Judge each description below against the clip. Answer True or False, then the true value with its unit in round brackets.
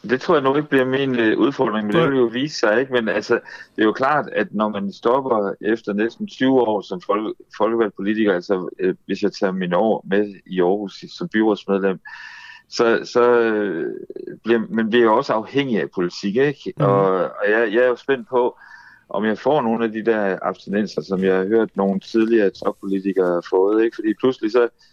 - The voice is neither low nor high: False (110 Hz)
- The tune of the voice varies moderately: True (3.7 semitones)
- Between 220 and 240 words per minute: False (200 wpm)